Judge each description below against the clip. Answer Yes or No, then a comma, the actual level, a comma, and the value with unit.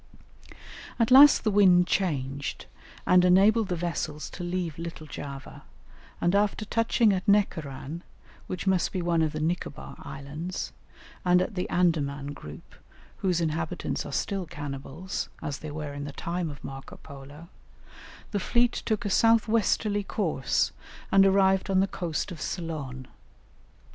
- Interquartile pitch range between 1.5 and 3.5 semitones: No, average, 4.8 semitones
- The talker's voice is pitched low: No, medium, 175 Hz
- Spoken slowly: No, average, 150 wpm